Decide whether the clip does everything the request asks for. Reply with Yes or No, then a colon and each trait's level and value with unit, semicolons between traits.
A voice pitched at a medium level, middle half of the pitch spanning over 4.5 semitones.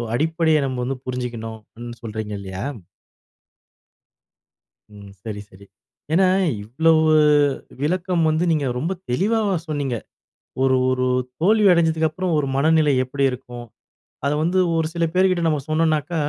Yes: medium, 155 Hz; average, 5.0 semitones